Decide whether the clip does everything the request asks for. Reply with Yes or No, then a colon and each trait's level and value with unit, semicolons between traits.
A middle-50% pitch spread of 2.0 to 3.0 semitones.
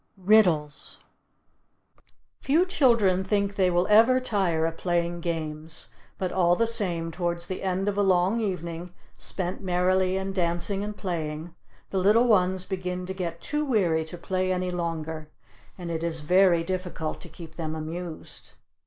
Yes: narrow, 2.5 semitones